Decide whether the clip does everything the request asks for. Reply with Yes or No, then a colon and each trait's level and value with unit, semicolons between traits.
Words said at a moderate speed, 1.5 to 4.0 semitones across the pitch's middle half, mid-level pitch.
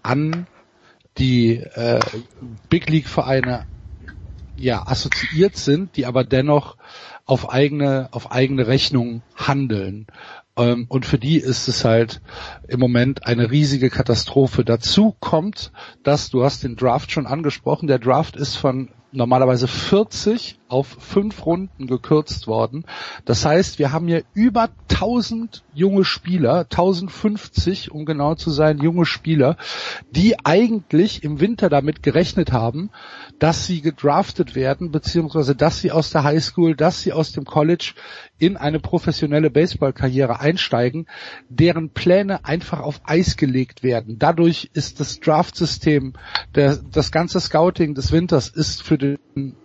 No: average, 135 wpm; average, 4.5 semitones; medium, 145 Hz